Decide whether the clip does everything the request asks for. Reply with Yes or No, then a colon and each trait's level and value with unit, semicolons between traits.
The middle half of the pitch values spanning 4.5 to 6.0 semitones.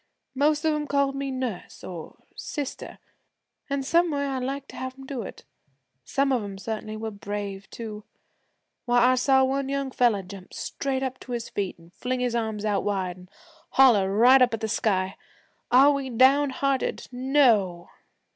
Yes: average, 4.8 semitones